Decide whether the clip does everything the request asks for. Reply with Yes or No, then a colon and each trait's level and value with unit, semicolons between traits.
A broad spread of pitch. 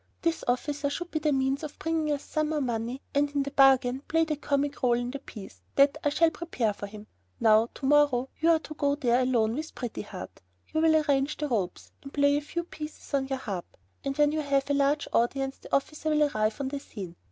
No: average, 3.2 semitones